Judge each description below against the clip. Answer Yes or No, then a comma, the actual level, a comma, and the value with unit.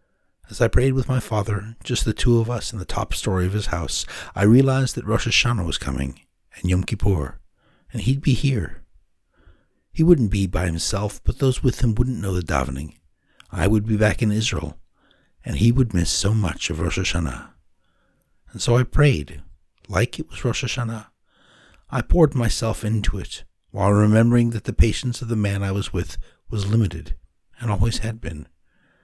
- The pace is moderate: Yes, average, 190 wpm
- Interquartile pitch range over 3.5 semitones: Yes, average, 5.3 semitones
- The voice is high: No, low, 105 Hz